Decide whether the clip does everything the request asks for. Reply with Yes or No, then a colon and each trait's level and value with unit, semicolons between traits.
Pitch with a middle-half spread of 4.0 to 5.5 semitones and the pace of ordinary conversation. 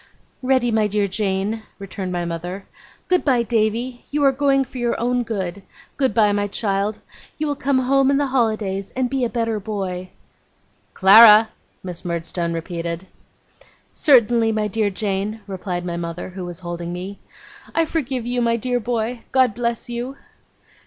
Yes: average, 4.5 semitones; average, 165 wpm